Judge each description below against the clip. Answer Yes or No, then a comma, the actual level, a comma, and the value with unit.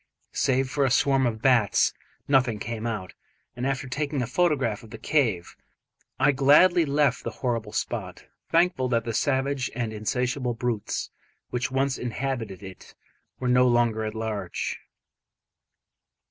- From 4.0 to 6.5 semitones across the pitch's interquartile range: No, average, 3.3 semitones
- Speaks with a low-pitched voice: Yes, low, 125 Hz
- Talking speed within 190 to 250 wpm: No, average, 145 wpm